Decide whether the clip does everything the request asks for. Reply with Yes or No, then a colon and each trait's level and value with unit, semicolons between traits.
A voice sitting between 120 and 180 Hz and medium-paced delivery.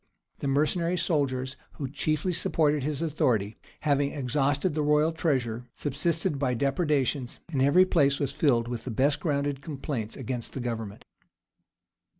Yes: medium, 140 Hz; average, 145 wpm